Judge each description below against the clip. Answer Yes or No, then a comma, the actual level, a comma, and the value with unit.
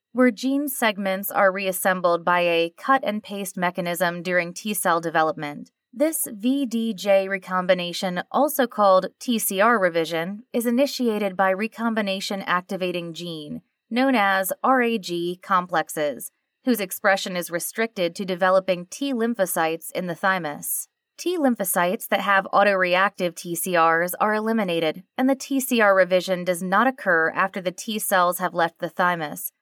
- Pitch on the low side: No, high, 190 Hz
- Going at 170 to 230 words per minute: No, slow, 135 wpm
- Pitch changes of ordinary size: Yes, average, 4.2 semitones